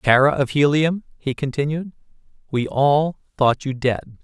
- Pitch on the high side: No, medium, 140 Hz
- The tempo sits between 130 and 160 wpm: Yes, average, 140 wpm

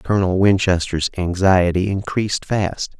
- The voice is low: Yes, very low, 95 Hz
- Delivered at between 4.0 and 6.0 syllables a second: Yes, 4.4 syllables/s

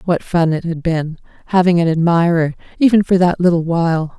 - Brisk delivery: No, average, 185 wpm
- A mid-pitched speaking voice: Yes, medium, 170 Hz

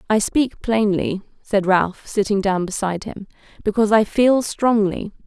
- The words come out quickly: No, average, 150 wpm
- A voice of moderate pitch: No, high, 205 Hz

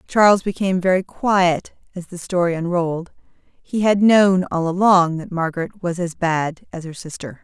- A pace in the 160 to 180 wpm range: Yes, average, 170 wpm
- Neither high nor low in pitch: Yes, medium, 180 Hz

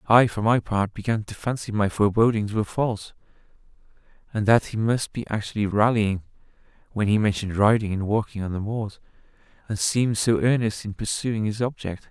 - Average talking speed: Yes, average, 175 wpm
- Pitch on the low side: Yes, low, 105 Hz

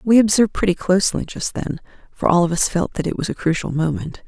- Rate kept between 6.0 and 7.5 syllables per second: Yes, 6.1 syllables/s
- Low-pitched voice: No, medium, 185 Hz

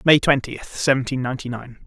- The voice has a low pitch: Yes, low, 130 Hz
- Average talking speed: Yes, average, 160 wpm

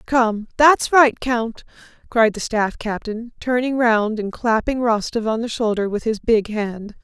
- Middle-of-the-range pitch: No, high, 230 Hz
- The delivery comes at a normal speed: Yes, average, 170 wpm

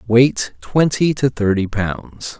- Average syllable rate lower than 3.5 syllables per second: Yes, 3.2 syllables/s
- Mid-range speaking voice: No, low, 115 Hz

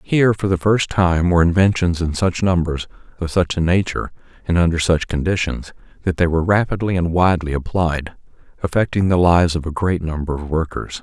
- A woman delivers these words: No, male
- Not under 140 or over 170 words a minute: No, average, 185 wpm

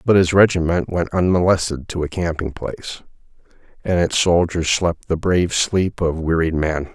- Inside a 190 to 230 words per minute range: No, average, 165 wpm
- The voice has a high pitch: No, very low, 85 Hz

